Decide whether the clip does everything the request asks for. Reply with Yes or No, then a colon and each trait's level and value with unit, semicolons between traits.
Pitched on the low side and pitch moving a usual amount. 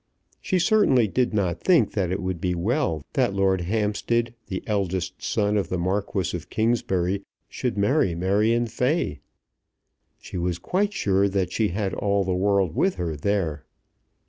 Yes: low, 100 Hz; average, 3.7 semitones